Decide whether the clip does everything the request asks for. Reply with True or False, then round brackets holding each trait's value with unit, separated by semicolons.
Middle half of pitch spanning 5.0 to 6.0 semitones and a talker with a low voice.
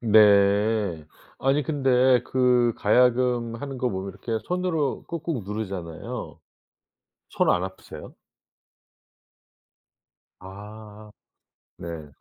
False (4.3 semitones; 110 Hz)